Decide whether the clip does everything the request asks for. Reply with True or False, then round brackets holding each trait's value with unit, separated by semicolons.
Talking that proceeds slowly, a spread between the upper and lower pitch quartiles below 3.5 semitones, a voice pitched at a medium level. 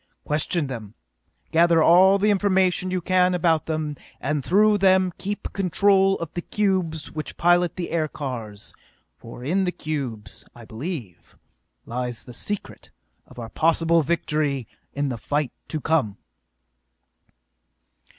False (130 wpm; 5.3 semitones; 160 Hz)